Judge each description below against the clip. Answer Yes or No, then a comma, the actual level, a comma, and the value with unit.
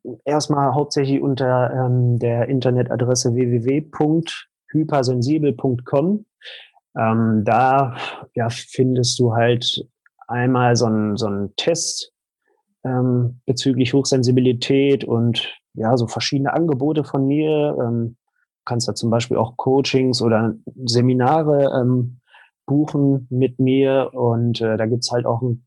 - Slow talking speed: Yes, slow, 115 wpm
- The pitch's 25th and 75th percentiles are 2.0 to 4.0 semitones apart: Yes, narrow, 2.5 semitones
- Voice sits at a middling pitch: No, low, 125 Hz